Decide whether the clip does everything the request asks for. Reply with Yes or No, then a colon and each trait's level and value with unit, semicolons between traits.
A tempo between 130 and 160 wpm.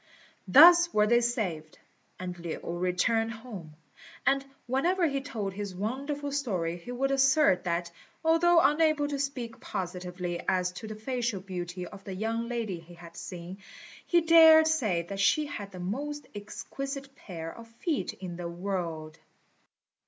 Yes: average, 150 wpm